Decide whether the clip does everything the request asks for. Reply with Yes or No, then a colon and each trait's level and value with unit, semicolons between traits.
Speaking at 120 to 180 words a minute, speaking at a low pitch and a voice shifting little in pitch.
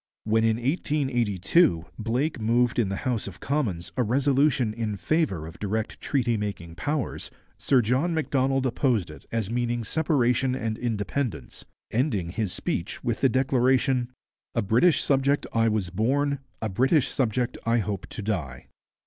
No: average, 150 wpm; low, 120 Hz; average, 4.0 semitones